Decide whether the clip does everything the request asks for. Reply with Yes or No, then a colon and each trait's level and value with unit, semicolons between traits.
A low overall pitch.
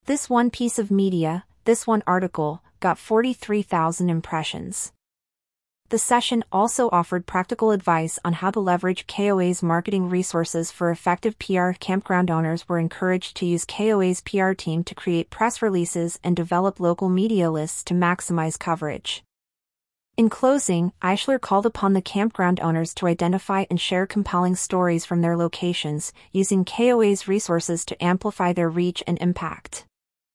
No: medium, 180 Hz